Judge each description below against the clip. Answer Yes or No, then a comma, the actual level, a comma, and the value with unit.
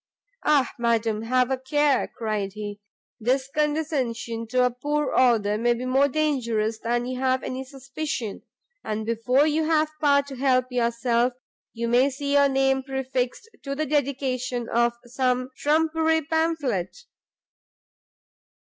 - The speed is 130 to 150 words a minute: Yes, average, 140 wpm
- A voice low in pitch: No, very high, 255 Hz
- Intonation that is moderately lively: Yes, average, 3.2 semitones